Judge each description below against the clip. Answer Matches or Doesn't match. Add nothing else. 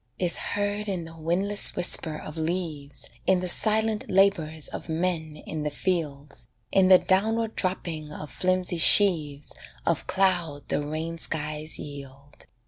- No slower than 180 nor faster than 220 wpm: Doesn't match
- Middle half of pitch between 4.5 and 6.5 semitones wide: Doesn't match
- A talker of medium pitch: Matches